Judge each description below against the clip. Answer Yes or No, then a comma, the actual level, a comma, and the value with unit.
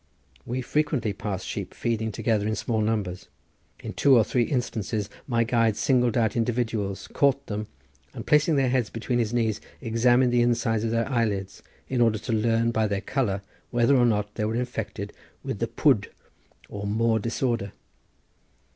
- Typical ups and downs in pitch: No, narrow, 2.2 semitones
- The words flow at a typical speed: Yes, average, 170 wpm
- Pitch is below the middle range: Yes, low, 115 Hz